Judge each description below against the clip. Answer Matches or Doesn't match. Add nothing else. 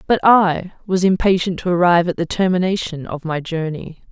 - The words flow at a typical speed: Matches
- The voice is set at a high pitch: Doesn't match